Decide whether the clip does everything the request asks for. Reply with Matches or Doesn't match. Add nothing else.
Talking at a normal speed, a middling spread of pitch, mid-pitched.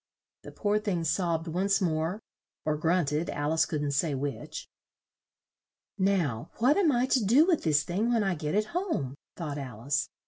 Doesn't match